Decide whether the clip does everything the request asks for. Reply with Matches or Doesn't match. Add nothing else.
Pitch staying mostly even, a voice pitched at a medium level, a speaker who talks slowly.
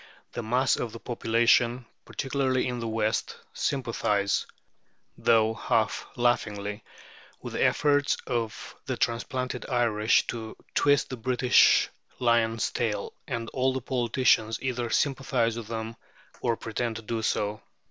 Doesn't match